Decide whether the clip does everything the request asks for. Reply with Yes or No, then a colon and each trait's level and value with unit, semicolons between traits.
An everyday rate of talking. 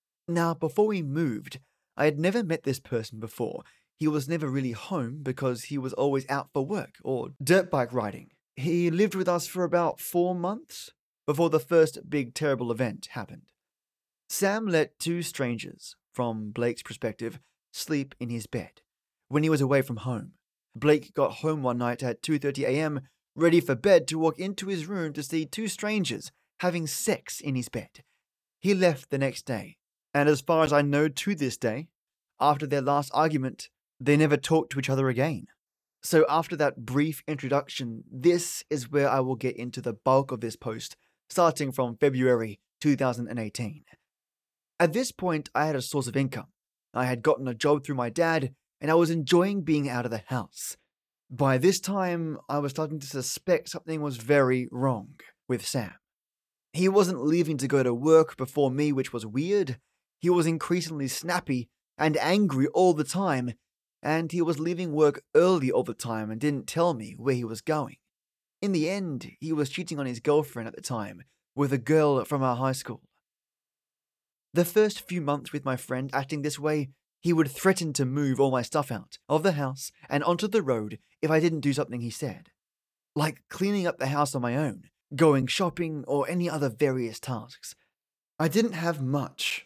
Yes: average, 185 wpm